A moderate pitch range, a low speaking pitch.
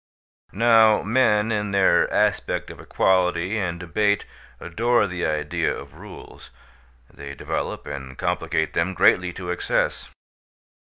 Yes: average, 3.9 semitones; very low, 95 Hz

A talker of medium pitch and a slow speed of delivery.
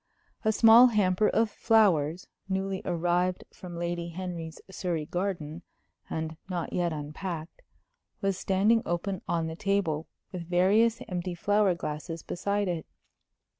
Yes: medium, 180 Hz; slow, 130 wpm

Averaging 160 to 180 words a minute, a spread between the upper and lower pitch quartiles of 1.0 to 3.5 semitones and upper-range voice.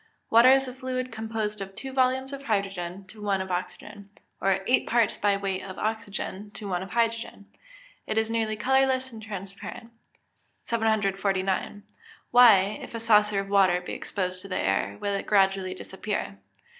Yes: average, 170 wpm; average, 3.0 semitones; high, 205 Hz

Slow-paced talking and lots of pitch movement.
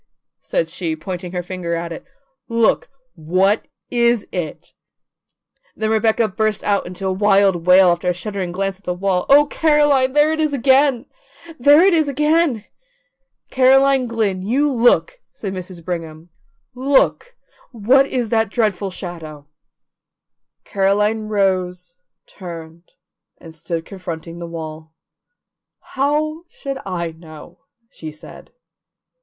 Yes: slow, 130 wpm; wide, 6.7 semitones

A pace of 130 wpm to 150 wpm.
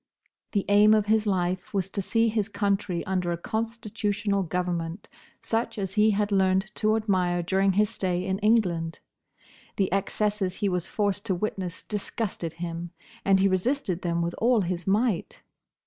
No: average, 165 wpm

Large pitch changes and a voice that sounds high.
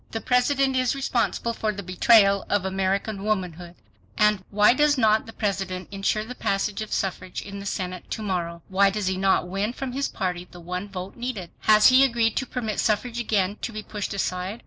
No: average, 3.2 semitones; high, 205 Hz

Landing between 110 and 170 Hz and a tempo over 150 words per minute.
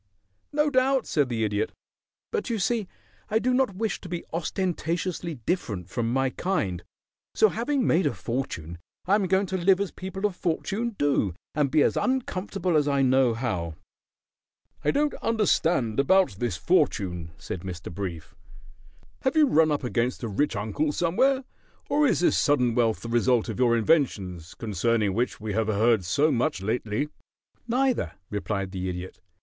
Yes: medium, 140 Hz; average, 165 wpm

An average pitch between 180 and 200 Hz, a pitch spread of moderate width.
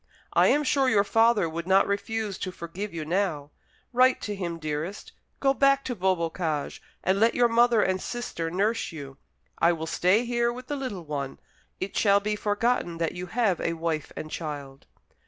No: high, 190 Hz; wide, 5.7 semitones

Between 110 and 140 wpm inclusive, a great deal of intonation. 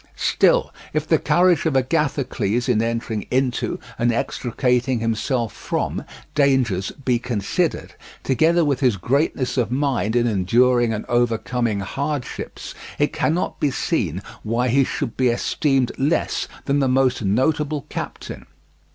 No: slow, 135 wpm; average, 3.2 semitones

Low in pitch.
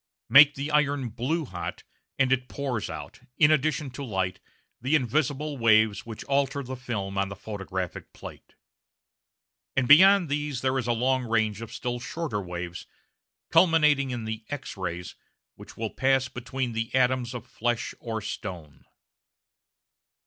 Yes: low, 125 Hz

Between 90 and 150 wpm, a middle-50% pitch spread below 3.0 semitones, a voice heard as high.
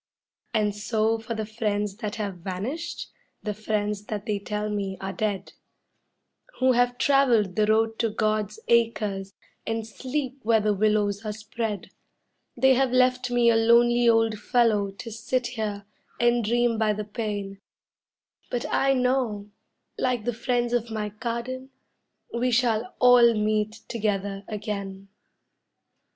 Yes: average, 140 wpm; narrow, 2.5 semitones; high, 220 Hz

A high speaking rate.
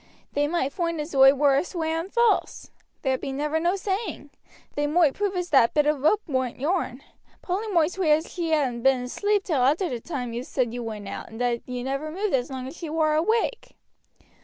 Yes: fast, 215 wpm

